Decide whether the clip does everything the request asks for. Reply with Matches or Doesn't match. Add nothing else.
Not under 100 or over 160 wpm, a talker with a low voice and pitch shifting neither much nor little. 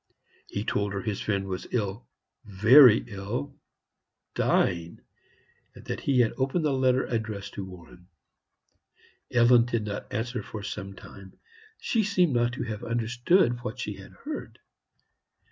Matches